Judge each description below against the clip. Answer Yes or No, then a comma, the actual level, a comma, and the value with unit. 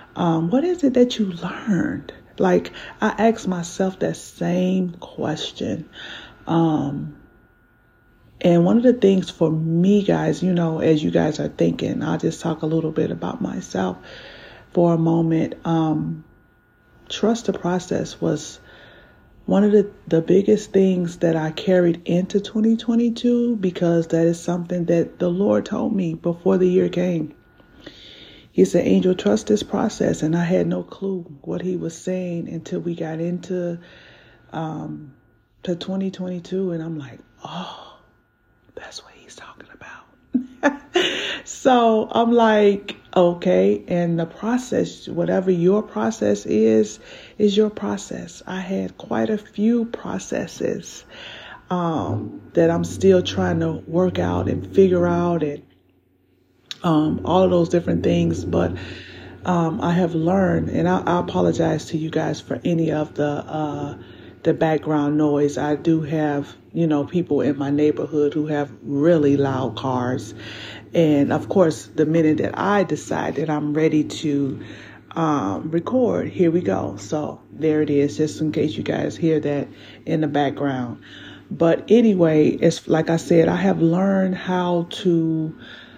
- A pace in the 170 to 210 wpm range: No, average, 150 wpm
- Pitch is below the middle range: No, medium, 165 Hz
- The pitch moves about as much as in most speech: Yes, average, 4.2 semitones